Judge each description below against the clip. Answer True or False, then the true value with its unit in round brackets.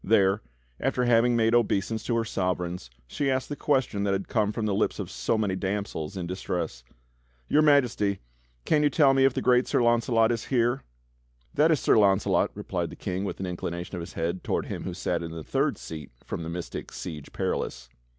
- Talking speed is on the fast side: True (210 wpm)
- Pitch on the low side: True (100 Hz)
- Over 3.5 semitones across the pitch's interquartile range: True (5.2 semitones)